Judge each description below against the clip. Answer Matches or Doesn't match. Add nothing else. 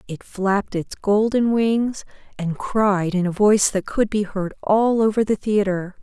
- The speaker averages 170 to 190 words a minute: Matches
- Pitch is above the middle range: Matches